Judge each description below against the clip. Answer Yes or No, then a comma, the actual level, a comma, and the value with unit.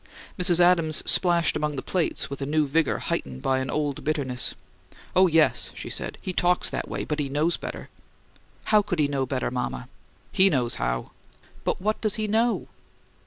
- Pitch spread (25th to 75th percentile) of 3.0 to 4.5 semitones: No, average, 4.9 semitones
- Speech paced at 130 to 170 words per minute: No, average, 185 wpm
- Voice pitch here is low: No, medium, 155 Hz